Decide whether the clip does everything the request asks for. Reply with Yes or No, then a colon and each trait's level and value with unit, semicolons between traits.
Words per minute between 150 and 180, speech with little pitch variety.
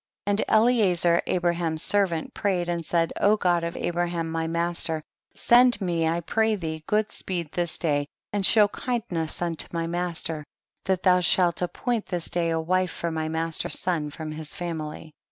Yes: average, 170 wpm; narrow, 2.2 semitones